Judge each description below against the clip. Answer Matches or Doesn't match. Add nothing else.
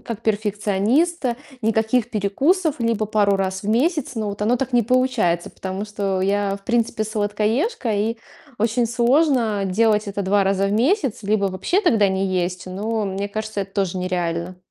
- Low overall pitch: Doesn't match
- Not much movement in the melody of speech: Doesn't match